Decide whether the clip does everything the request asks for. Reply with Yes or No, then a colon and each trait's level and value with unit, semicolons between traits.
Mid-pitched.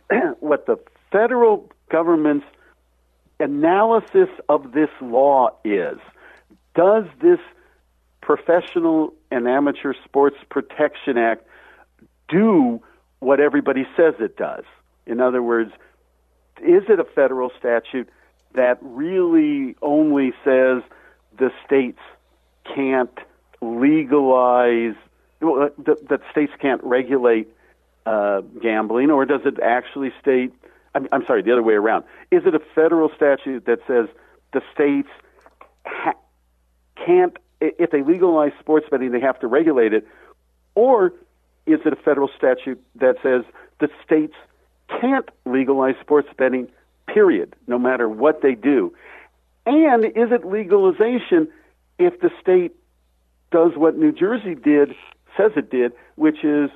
Yes: medium, 145 Hz